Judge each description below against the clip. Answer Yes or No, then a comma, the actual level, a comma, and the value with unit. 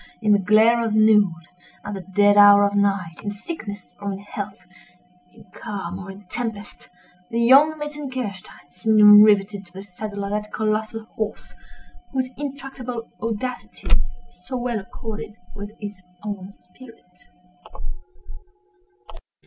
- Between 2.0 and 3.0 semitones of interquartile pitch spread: Yes, average, 2.7 semitones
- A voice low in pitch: No, high, 210 Hz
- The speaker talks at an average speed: No, slow, 120 wpm